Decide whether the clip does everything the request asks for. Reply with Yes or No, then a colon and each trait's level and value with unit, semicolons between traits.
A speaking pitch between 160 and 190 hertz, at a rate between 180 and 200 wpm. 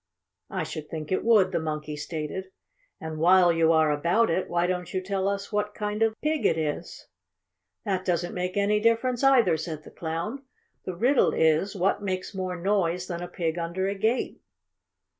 Yes: medium, 185 Hz; average, 185 wpm